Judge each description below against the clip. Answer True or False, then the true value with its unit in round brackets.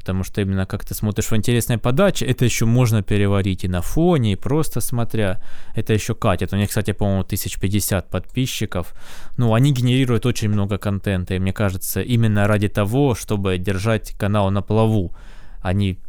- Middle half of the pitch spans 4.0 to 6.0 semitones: False (3.0 semitones)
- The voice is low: True (105 Hz)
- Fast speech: True (170 wpm)